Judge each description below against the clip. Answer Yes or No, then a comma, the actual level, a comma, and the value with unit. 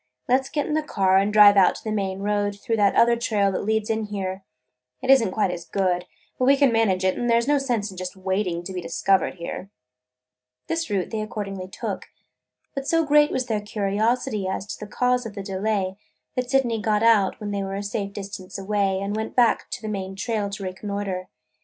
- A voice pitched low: No, high, 205 Hz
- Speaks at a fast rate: Yes, fast, 225 wpm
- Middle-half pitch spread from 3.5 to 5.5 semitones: No, average, 3.1 semitones